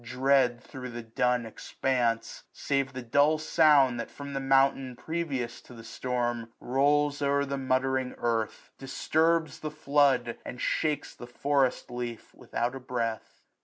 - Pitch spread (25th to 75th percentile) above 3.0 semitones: No, average, 2.7 semitones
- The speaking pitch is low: Yes, low, 130 Hz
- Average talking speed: Yes, average, 145 wpm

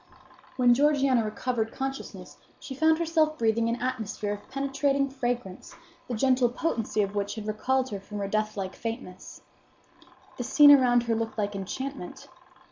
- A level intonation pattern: No, average, 4.0 semitones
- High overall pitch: Yes, high, 240 Hz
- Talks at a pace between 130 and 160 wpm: Yes, average, 150 wpm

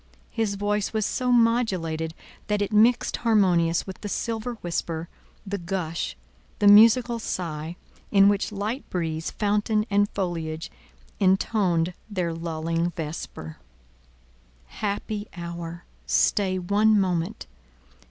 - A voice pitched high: Yes, high, 195 Hz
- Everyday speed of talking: No, slow, 110 wpm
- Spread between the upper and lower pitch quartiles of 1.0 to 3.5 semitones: No, average, 4.0 semitones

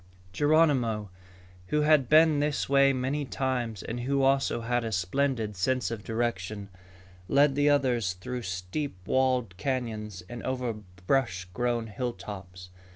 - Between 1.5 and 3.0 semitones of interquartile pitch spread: No, average, 4.4 semitones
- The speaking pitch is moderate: No, low, 120 Hz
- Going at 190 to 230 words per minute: No, slow, 135 wpm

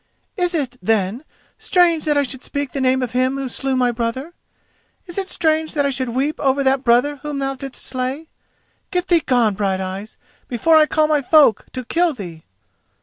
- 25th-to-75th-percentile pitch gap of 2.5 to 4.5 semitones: Yes, average, 3.9 semitones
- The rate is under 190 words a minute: No, average, 195 wpm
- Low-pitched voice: No, very high, 270 Hz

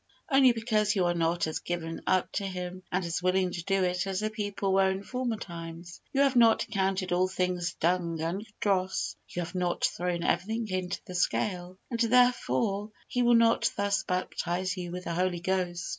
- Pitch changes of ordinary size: Yes, average, 3.0 semitones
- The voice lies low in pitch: No, medium, 185 Hz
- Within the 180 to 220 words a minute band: Yes, average, 195 wpm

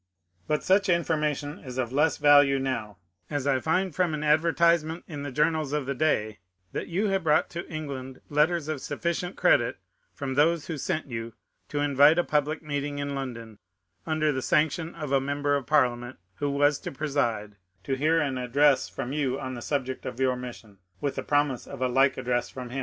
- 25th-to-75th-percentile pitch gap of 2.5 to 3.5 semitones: Yes, average, 3.0 semitones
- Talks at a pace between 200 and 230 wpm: Yes, fast, 205 wpm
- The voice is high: No, medium, 145 Hz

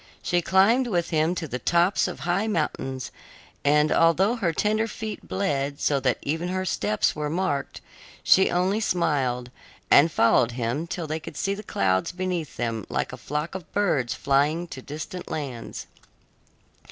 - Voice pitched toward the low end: No, medium, 160 Hz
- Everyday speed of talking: Yes, average, 165 wpm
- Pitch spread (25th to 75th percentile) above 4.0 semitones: Yes, average, 5.2 semitones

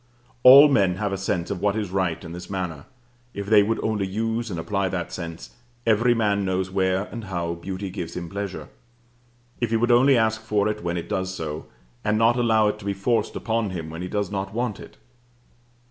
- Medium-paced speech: No, fast, 210 wpm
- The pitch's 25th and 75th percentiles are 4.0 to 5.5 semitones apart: No, average, 3.3 semitones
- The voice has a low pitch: Yes, low, 100 Hz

